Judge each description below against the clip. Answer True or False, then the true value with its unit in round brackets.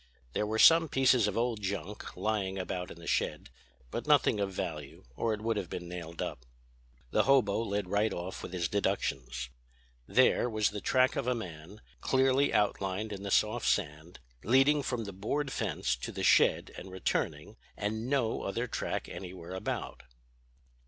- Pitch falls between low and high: False (105 Hz)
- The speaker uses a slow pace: False (170 wpm)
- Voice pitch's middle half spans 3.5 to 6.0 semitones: True (4.1 semitones)